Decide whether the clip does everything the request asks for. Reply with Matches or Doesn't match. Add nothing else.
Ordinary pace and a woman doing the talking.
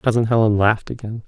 Doesn't match